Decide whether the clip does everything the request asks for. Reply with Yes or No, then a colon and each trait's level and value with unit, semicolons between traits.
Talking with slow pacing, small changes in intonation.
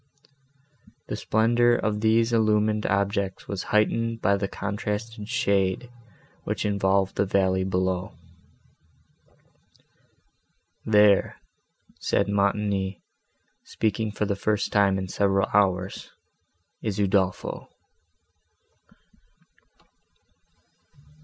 Yes: slow, 85 wpm; narrow, 1.8 semitones